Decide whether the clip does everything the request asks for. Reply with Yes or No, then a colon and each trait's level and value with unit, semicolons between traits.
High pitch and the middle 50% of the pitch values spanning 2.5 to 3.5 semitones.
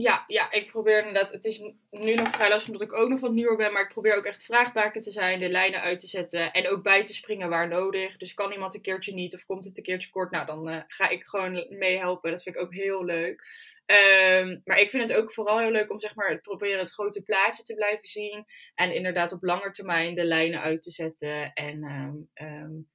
Yes: high, 195 Hz; average, 3.2 semitones